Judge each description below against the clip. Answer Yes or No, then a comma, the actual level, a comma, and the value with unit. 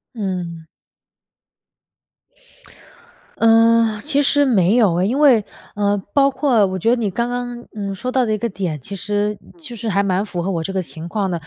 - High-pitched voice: Yes, high, 210 Hz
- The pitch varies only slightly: No, average, 4.1 semitones